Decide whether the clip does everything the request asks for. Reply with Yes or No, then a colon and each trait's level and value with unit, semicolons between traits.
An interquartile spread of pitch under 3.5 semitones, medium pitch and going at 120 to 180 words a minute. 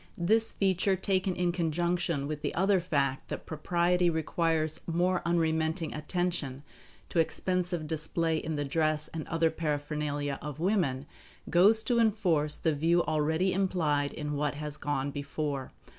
Yes: average, 3.1 semitones; medium, 160 Hz; average, 145 wpm